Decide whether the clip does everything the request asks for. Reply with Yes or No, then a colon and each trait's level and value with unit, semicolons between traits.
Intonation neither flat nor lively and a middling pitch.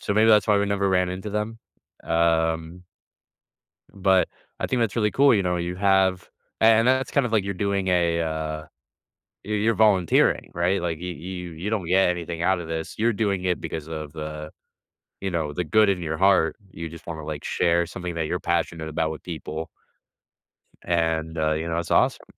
No: average, 3.4 semitones; very low, 90 Hz